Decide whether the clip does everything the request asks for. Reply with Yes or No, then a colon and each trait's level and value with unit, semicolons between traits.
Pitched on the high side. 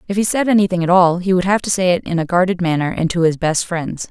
No: medium, 180 Hz